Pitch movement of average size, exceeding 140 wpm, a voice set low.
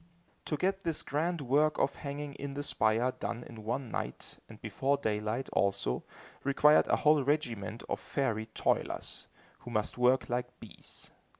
Yes: average, 4.2 semitones; average, 160 wpm; low, 130 Hz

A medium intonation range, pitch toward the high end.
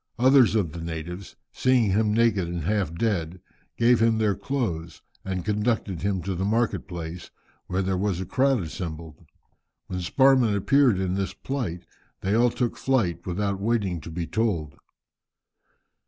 No: average, 4.9 semitones; low, 100 Hz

